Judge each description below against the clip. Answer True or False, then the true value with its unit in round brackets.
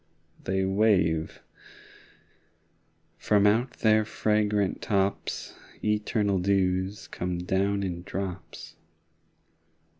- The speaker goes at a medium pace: False (80 wpm)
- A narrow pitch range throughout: True (2.2 semitones)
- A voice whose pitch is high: False (100 Hz)